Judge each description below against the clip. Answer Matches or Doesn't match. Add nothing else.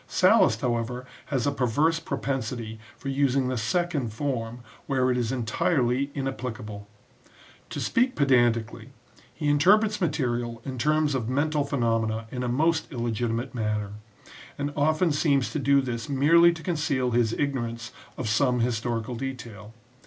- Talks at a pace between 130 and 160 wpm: Matches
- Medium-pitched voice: Doesn't match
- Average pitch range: Matches